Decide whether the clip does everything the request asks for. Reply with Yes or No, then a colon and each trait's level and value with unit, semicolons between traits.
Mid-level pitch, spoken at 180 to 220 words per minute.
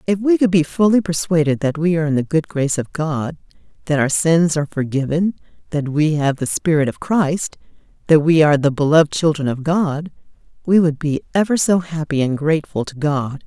Yes: medium, 160 Hz; average, 200 wpm